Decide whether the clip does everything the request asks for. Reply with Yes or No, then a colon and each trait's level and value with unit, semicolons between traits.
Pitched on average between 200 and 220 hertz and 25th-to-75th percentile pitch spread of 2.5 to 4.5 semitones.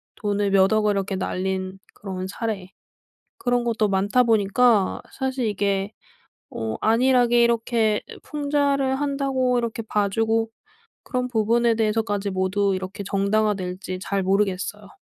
Yes: high, 210 Hz; average, 3.5 semitones